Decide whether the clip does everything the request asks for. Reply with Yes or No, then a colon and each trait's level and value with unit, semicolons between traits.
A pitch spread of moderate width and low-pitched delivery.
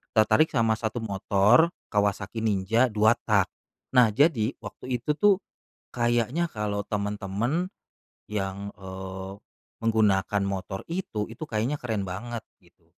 Yes: average, 3.3 semitones; low, 110 Hz